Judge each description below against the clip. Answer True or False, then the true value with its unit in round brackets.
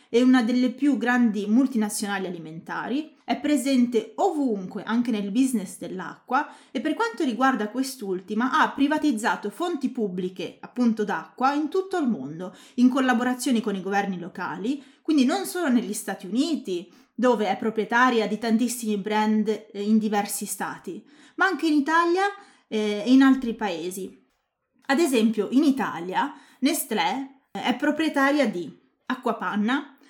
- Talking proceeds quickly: False (135 wpm)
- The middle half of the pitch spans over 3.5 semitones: True (4.9 semitones)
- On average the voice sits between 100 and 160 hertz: False (245 Hz)